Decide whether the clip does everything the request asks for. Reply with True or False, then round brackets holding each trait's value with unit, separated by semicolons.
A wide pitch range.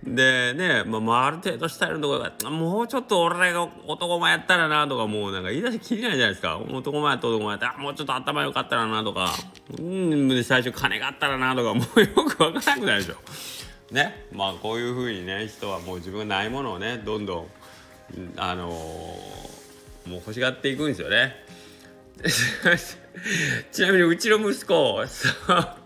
True (8.4 semitones)